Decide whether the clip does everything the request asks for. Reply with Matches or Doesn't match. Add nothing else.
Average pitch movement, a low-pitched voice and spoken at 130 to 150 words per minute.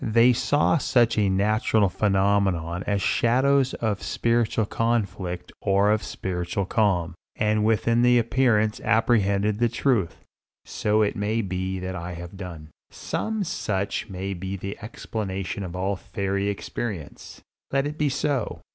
Matches